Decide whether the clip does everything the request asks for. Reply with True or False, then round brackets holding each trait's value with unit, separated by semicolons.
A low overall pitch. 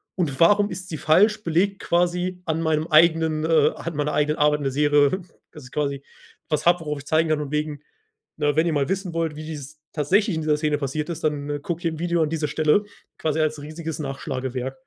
False (155 Hz)